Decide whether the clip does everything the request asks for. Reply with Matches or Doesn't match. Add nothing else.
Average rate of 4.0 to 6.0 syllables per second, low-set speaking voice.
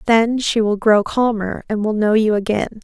Doesn't match